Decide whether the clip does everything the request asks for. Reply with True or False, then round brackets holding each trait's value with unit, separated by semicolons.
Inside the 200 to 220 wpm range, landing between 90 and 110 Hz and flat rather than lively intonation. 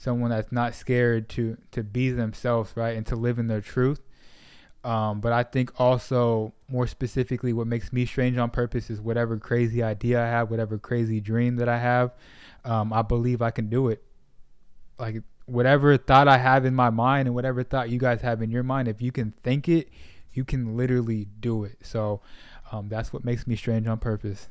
False (205 wpm; 120 Hz; 1.9 semitones)